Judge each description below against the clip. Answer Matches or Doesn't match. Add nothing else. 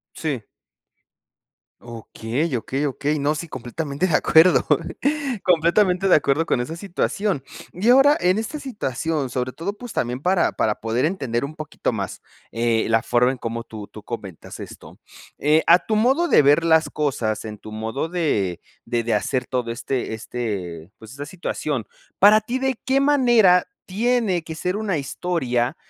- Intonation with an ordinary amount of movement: Doesn't match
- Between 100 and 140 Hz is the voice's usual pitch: Doesn't match